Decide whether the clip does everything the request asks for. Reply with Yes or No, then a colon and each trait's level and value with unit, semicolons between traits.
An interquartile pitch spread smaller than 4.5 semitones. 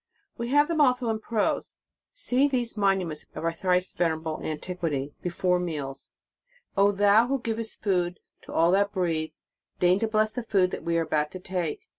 No: average, 5.0 semitones